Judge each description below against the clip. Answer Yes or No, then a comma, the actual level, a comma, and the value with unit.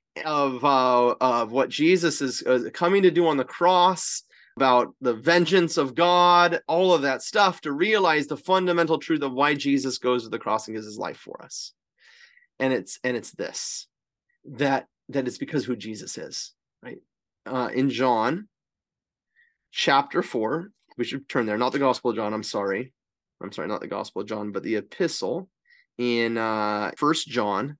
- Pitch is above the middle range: No, low, 135 Hz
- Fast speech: No, average, 180 wpm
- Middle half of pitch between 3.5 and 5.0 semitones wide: No, wide, 5.6 semitones